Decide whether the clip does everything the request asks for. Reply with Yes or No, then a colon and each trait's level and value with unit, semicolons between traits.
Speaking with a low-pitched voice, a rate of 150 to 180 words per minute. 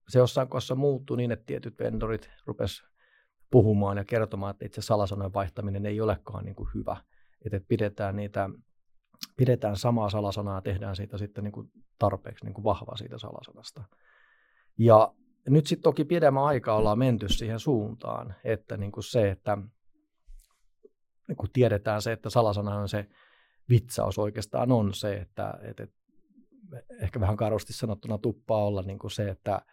Yes: low, 110 Hz; fast, 155 wpm